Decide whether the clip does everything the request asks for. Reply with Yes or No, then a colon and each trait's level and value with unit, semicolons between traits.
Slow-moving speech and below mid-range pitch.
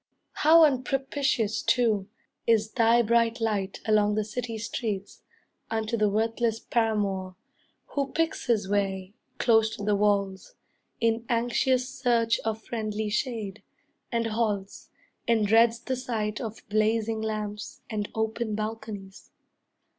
No: slow, 125 wpm; high, 220 Hz